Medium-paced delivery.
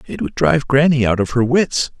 No: fast, 240 wpm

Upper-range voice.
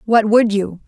Yes: high, 210 Hz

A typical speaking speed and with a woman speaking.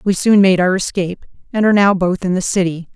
No: fast, 245 wpm; female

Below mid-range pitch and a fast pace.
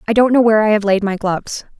No: high, 210 Hz; fast, 300 wpm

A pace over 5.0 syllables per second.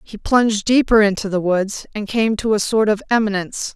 Yes: 5.4 syllables/s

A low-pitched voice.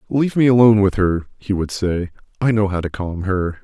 Yes: low, 100 Hz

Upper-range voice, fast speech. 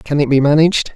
No: medium, 145 Hz; fast, 250 wpm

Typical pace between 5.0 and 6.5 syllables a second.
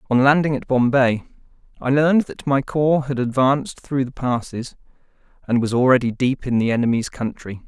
Yes: 5.3 syllables/s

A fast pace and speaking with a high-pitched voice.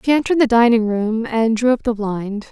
Yes: fast, 240 wpm; high, 230 Hz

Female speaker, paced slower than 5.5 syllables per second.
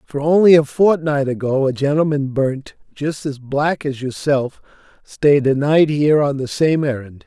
No: male; 4.4 syllables/s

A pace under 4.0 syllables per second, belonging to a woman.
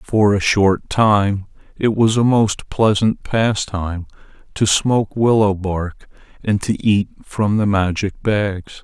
No: 3.6 syllables/s; male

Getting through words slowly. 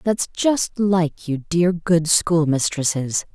Yes: slow, 125 wpm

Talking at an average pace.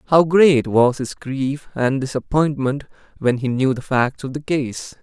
Yes: average, 180 wpm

